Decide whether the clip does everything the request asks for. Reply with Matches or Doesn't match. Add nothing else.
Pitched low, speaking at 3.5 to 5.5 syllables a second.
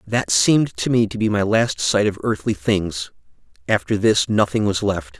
Matches